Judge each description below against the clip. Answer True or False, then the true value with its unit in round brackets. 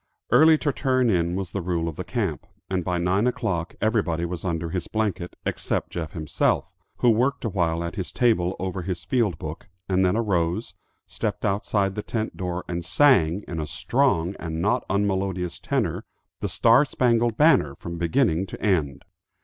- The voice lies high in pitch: False (95 Hz)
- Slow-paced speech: False (175 wpm)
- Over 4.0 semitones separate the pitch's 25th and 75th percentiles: True (4.8 semitones)